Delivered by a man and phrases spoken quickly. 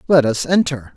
No: male; average, 190 wpm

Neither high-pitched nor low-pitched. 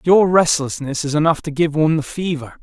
Yes: medium, 155 Hz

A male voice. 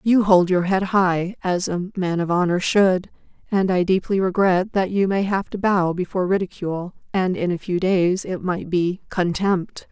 No: female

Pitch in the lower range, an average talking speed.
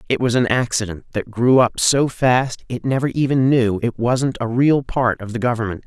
No: low, 120 Hz; fast, 215 wpm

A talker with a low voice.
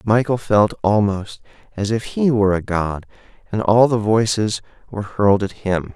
Yes: low, 105 Hz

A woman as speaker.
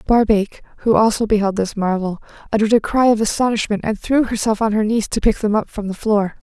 Yes: female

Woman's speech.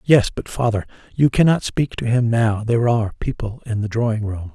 No: male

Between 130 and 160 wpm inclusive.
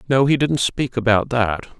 No: average, 200 wpm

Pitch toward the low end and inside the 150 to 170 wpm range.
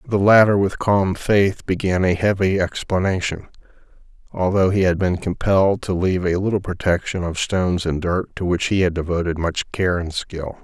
No: very low, 95 Hz; average, 180 wpm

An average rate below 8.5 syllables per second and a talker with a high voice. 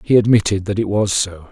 No: 5.7 syllables/s; low, 100 Hz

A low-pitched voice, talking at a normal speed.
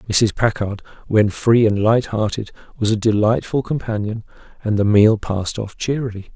Yes: low, 110 Hz; average, 150 wpm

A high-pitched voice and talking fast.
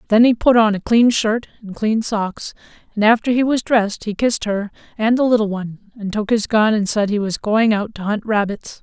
Yes: high, 215 Hz; fast, 240 wpm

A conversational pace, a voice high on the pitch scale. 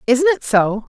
Yes: average, 190 wpm; very high, 260 Hz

